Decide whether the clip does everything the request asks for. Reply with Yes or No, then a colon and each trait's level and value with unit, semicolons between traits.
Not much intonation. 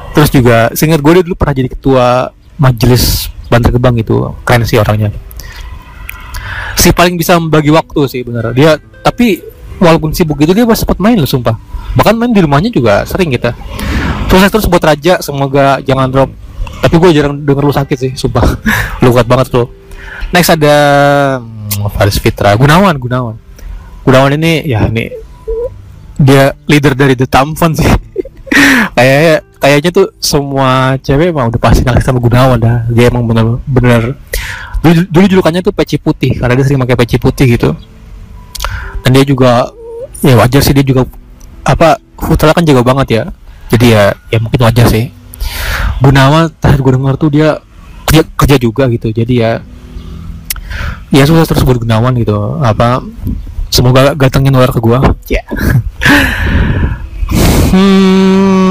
No: average, 5.1 semitones